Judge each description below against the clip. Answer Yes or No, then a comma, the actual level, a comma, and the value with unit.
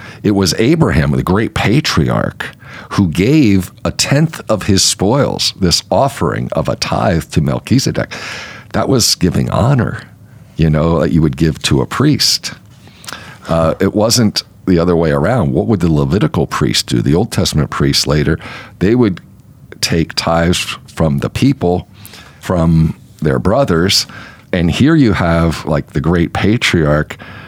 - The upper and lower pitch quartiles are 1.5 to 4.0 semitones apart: No, average, 4.7 semitones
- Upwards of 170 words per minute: No, average, 150 wpm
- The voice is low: Yes, very low, 95 Hz